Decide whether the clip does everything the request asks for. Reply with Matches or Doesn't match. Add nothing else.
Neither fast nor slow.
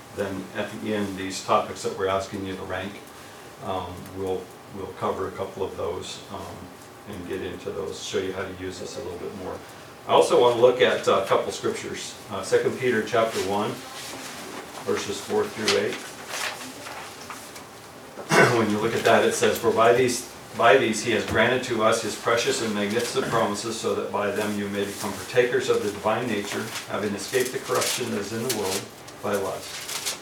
Matches